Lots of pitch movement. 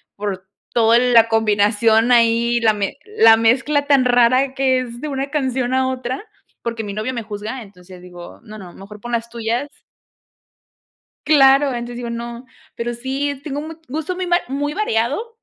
No: average, 3.3 semitones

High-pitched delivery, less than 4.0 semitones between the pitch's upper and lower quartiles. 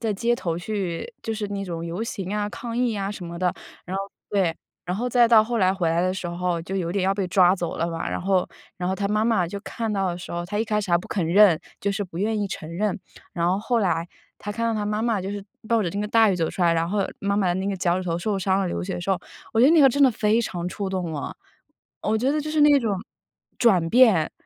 Yes: high, 195 Hz; average, 3.6 semitones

